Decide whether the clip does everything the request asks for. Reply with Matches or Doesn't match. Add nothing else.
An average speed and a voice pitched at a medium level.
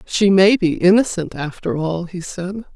Matches